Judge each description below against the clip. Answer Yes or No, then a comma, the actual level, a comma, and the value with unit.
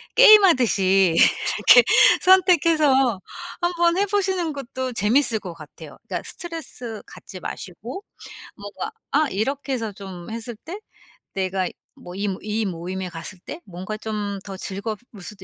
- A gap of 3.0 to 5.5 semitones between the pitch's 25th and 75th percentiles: No, wide, 8.4 semitones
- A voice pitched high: Yes, high, 220 Hz